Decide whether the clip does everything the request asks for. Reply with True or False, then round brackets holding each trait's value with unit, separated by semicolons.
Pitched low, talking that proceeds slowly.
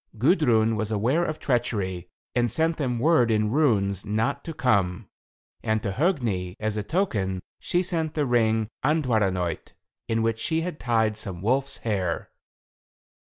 False (115 Hz; 150 wpm)